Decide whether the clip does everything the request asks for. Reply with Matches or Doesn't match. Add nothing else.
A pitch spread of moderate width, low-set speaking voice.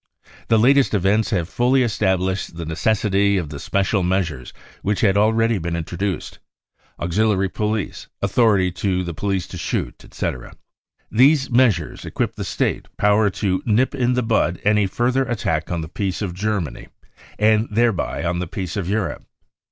Matches